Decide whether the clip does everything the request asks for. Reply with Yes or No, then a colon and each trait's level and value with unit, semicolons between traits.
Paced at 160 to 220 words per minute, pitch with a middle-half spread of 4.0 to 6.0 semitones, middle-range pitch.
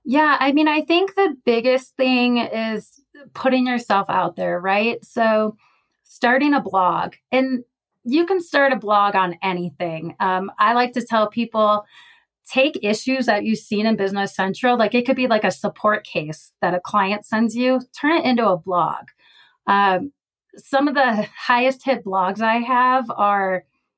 No: average, 170 wpm; average, 4.6 semitones; high, 230 Hz